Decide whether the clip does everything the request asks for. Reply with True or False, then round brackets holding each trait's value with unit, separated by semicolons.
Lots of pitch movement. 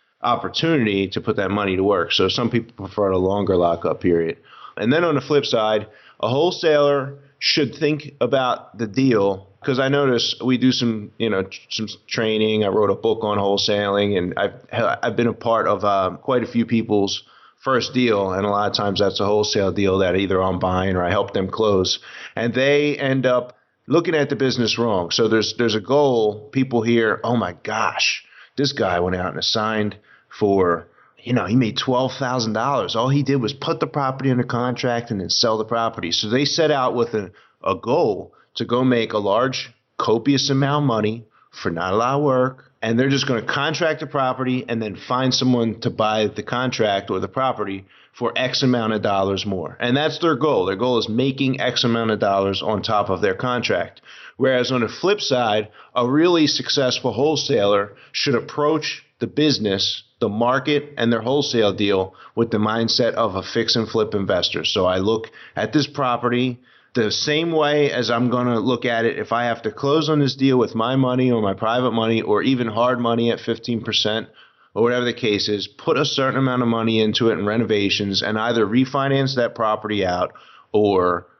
False (3.9 semitones)